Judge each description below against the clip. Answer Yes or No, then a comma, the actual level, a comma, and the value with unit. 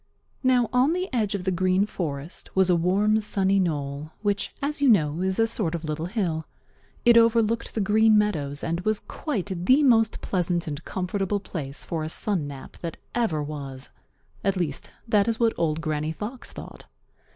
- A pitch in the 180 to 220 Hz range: Yes, high, 190 Hz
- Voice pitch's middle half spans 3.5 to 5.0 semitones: No, wide, 5.5 semitones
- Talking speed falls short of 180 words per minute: No, average, 185 wpm